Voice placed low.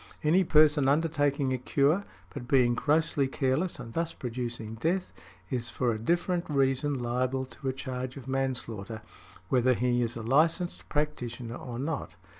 Yes: low, 130 Hz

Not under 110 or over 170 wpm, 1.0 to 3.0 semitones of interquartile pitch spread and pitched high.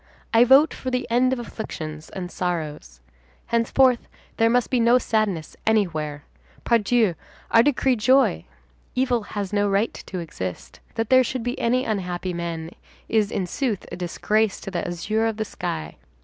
No: average, 165 wpm; wide, 5.5 semitones; high, 215 Hz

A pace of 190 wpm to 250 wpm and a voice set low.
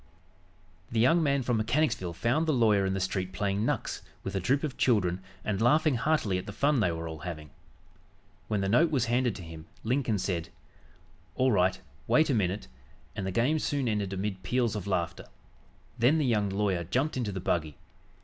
Yes: average, 195 wpm; low, 105 Hz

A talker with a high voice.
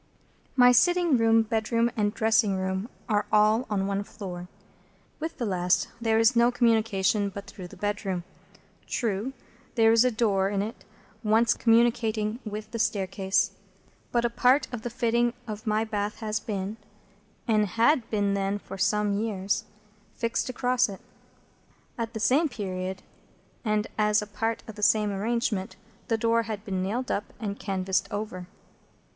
Yes: high, 215 Hz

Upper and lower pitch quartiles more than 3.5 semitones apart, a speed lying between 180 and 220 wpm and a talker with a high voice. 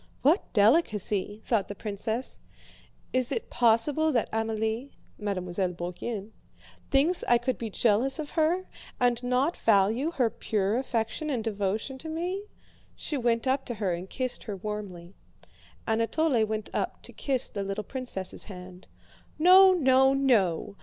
No: average, 4.7 semitones; average, 145 wpm; high, 230 Hz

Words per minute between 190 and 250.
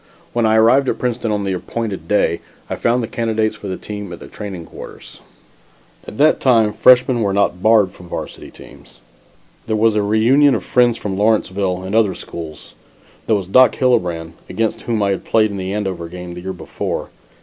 Yes: average, 195 wpm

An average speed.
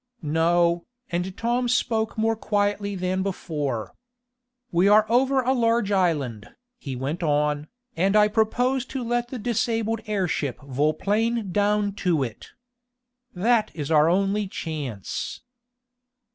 No: slow, 130 wpm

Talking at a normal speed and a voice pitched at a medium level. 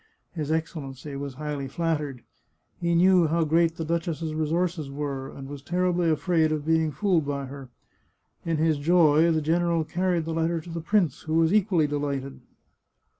Yes: average, 170 wpm; medium, 160 Hz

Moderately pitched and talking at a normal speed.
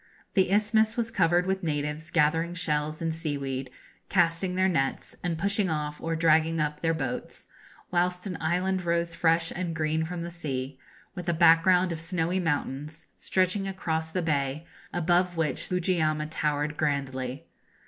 Yes: medium, 165 Hz; average, 155 wpm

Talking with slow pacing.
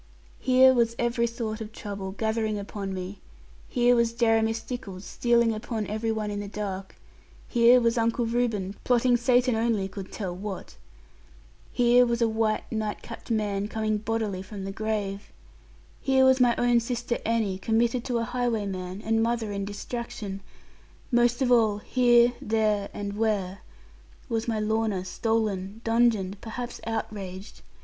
No: average, 150 wpm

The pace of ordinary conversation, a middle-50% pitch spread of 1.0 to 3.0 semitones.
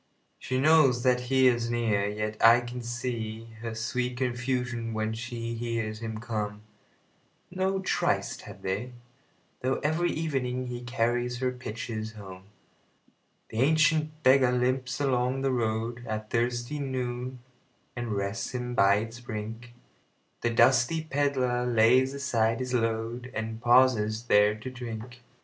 No: slow, 120 wpm; narrow, 2.4 semitones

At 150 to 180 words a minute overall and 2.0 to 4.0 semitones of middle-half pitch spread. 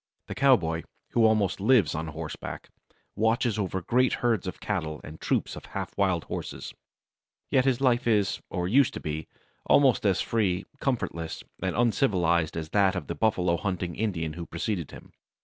No: average, 165 wpm; average, 5.3 semitones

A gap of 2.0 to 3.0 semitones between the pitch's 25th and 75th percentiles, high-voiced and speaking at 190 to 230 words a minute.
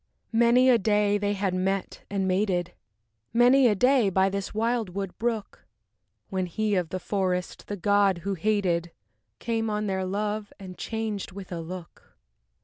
No: narrow, 2.6 semitones; high, 200 Hz; average, 160 wpm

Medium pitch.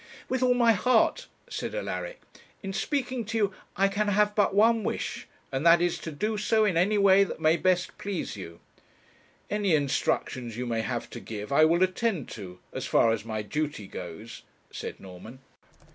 Yes: medium, 180 Hz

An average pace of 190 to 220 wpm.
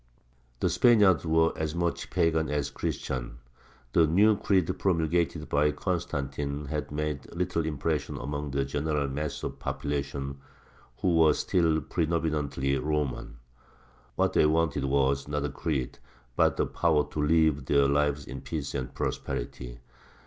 No: average, 140 wpm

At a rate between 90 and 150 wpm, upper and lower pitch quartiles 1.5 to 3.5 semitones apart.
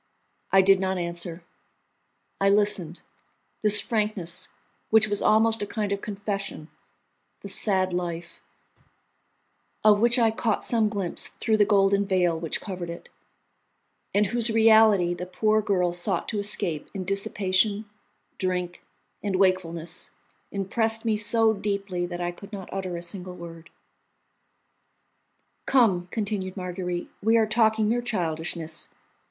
Yes: slow, 135 wpm; average, 3.2 semitones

